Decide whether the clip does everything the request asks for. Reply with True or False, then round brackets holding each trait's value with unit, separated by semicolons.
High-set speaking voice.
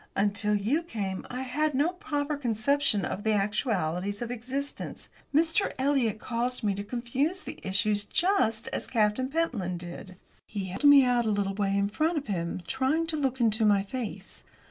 True (230 Hz)